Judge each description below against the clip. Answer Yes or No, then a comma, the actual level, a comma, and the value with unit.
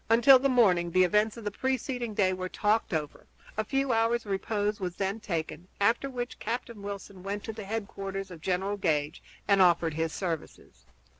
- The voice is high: Yes, high, 200 Hz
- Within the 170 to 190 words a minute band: Yes, average, 180 wpm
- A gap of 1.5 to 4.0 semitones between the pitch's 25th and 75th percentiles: Yes, average, 3.7 semitones